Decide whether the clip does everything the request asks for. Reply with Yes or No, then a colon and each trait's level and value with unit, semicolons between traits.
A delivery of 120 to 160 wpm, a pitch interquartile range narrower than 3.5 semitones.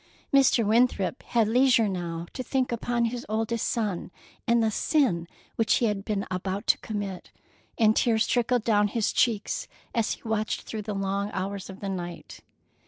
No: average, 170 wpm; average, 3.0 semitones